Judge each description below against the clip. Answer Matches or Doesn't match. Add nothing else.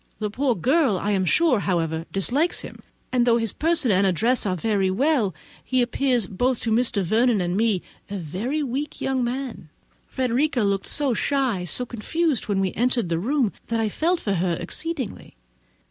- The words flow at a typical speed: Matches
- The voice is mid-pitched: Doesn't match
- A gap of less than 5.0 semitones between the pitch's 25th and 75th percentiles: Doesn't match